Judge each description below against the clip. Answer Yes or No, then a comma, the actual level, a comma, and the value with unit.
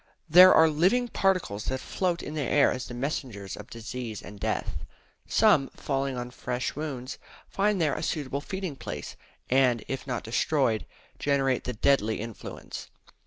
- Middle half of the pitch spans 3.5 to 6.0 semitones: Yes, average, 4.2 semitones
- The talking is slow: No, average, 160 wpm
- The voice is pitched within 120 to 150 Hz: Yes, low, 135 Hz